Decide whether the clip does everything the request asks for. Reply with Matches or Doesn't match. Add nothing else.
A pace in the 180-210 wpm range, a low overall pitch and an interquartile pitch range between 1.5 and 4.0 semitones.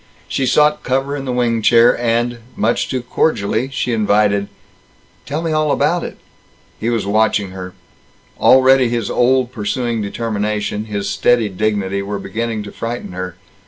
Doesn't match